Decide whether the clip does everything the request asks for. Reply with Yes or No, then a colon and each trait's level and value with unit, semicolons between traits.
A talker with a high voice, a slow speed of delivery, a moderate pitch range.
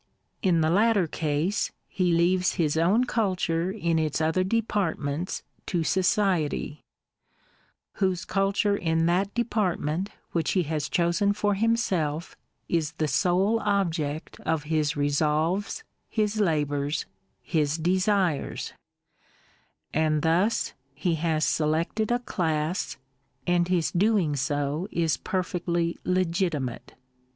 No: medium, 170 Hz; slow, 115 wpm; average, 3.8 semitones